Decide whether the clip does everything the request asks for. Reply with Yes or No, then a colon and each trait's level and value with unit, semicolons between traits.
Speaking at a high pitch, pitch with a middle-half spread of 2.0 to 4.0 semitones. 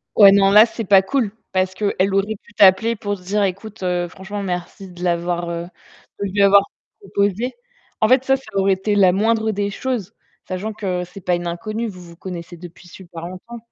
Yes: high, 195 Hz; average, 2.7 semitones